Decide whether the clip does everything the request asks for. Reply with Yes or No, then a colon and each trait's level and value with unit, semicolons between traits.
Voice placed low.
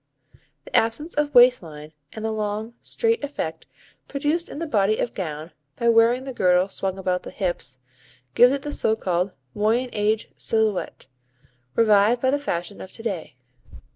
No: high, 220 Hz